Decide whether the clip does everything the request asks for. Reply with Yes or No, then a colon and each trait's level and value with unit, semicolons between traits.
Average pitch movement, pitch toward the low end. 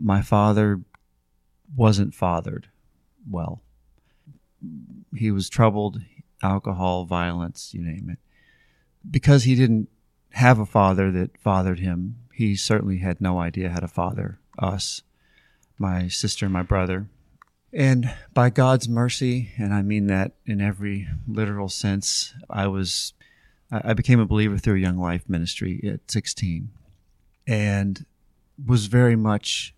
Yes: average, 3.9 semitones; low, 100 Hz